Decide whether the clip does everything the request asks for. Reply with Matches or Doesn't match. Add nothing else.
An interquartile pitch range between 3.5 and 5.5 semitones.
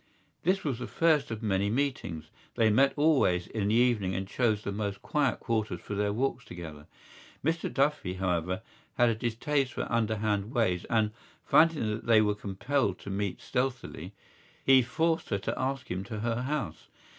Matches